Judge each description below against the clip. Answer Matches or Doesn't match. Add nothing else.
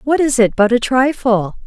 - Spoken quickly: Matches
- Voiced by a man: Doesn't match